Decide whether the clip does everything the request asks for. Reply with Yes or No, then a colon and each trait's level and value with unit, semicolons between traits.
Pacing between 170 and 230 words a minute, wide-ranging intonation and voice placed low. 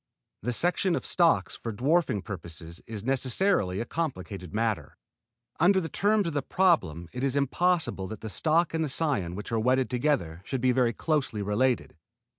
Yes: average, 175 wpm; wide, 7.9 semitones; low, 125 Hz